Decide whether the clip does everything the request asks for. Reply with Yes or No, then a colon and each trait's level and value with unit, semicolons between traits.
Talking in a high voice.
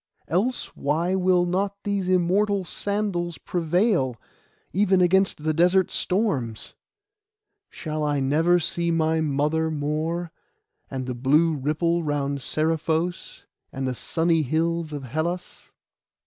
No: medium, 165 Hz